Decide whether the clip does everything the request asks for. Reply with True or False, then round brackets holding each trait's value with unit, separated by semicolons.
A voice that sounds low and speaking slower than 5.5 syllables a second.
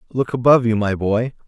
False (115 Hz; 6.0 syllables/s)